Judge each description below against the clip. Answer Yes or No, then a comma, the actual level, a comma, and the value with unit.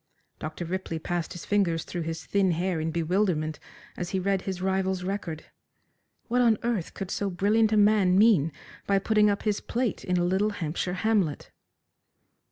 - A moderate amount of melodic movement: Yes, average, 3.2 semitones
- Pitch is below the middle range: No, high, 190 Hz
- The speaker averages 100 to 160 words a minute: No, average, 175 wpm